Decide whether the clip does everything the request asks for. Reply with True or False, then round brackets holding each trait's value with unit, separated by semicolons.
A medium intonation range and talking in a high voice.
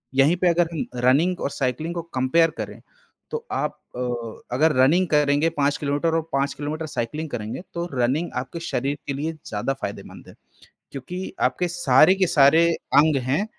False (3.6 semitones; 150 Hz)